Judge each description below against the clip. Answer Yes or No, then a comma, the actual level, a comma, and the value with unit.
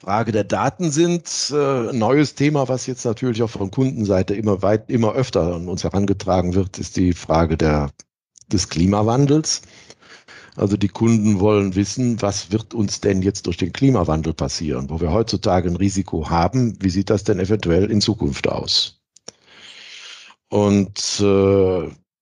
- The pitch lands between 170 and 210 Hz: No, low, 100 Hz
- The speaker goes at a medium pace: Yes, average, 155 wpm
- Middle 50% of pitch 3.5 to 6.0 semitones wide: Yes, average, 3.8 semitones